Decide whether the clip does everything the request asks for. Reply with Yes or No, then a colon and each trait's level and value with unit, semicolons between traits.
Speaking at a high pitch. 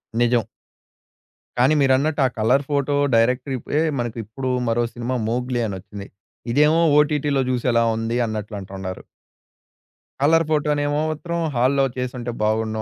No: low, 125 Hz